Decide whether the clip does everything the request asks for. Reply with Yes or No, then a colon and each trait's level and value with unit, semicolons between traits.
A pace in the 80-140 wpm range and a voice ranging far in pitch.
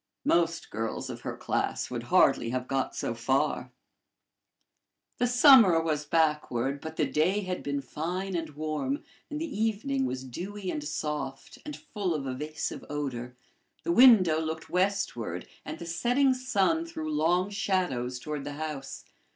No: average, 150 wpm; wide, 5.8 semitones